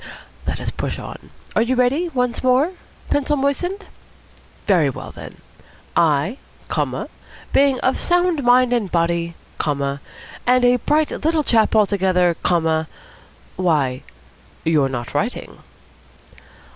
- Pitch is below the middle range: No, high, 230 Hz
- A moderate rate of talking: No, slow, 120 wpm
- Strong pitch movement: Yes, wide, 8.3 semitones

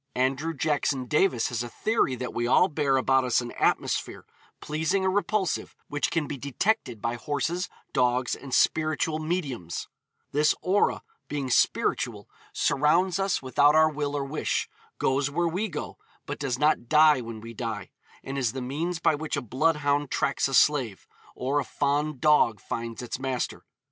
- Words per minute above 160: Yes, average, 170 wpm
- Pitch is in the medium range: Yes, medium, 145 Hz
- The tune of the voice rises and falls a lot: No, average, 3.8 semitones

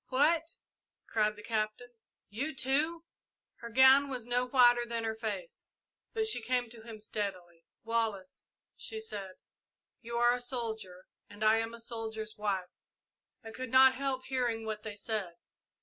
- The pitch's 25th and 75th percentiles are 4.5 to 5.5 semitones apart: No, average, 3.2 semitones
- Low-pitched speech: No, high, 230 Hz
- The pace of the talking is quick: No, average, 155 wpm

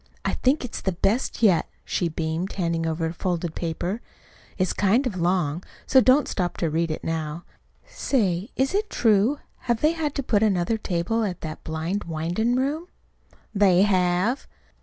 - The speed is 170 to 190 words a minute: Yes, average, 175 wpm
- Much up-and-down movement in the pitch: Yes, wide, 5.8 semitones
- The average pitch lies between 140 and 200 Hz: Yes, medium, 185 Hz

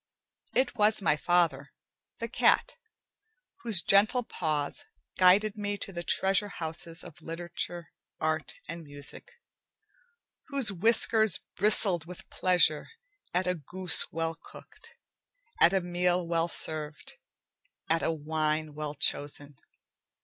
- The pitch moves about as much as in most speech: Yes, average, 3.8 semitones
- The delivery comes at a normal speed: No, slow, 120 wpm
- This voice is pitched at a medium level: Yes, medium, 175 Hz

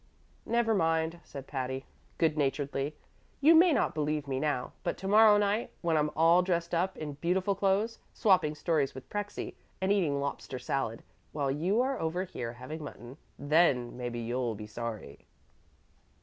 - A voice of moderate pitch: Yes, medium, 155 Hz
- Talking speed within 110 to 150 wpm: No, average, 165 wpm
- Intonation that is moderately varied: No, wide, 6.0 semitones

